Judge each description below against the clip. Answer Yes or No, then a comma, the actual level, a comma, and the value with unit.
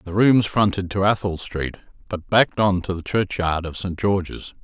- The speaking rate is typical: Yes, average, 195 wpm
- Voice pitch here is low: Yes, very low, 95 Hz